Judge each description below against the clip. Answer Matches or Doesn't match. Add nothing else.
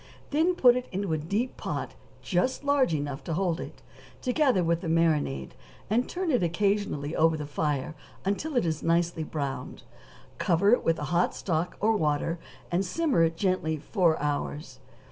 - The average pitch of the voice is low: Doesn't match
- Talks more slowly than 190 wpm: Matches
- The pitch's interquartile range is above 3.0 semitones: Matches